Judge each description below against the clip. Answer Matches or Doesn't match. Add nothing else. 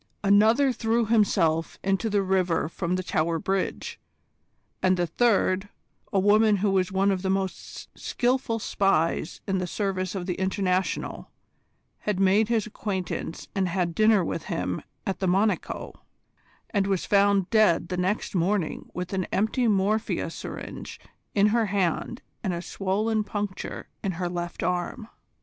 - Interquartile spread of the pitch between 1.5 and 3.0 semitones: Matches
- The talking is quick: Doesn't match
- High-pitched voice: Matches